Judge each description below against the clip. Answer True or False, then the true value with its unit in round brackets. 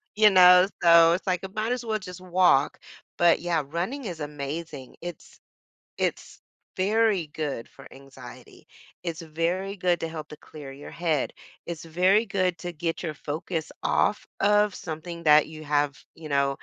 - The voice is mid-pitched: True (170 Hz)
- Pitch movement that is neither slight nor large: True (3.2 semitones)